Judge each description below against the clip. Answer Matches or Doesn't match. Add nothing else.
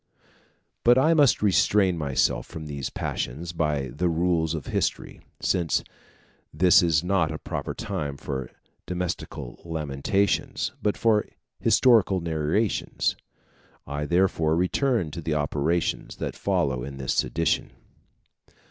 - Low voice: Matches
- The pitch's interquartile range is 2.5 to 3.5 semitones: Doesn't match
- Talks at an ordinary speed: Doesn't match